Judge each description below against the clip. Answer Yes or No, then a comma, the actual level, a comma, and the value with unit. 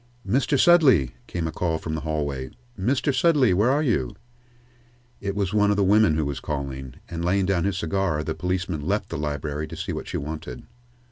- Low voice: Yes, very low, 90 Hz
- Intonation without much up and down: No, average, 5.3 semitones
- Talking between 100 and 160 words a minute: No, average, 200 wpm